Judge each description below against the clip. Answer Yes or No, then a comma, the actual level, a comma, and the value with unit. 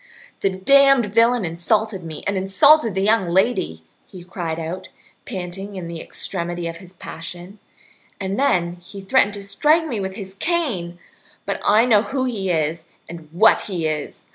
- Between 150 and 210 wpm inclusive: Yes, average, 165 wpm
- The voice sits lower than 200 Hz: Yes, high, 190 Hz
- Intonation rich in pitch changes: No, average, 4.3 semitones